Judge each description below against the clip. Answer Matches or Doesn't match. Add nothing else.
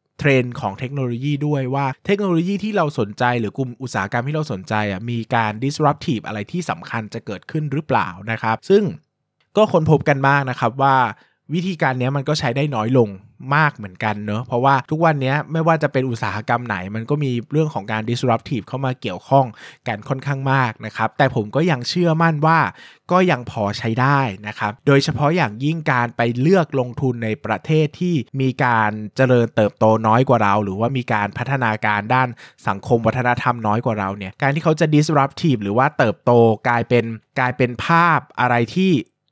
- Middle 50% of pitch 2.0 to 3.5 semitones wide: Doesn't match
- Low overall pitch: Matches